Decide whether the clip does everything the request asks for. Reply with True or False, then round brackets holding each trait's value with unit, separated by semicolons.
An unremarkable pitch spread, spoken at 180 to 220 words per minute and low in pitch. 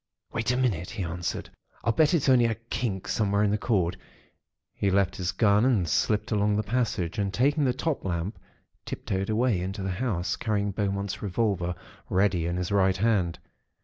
True (3.6 semitones; 185 wpm; 100 Hz)